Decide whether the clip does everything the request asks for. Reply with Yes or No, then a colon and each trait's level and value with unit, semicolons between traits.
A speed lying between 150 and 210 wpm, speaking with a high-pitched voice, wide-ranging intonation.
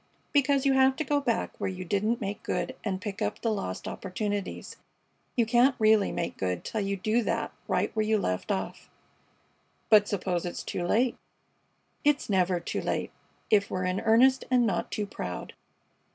No: average, 180 wpm; high, 215 Hz; average, 4.3 semitones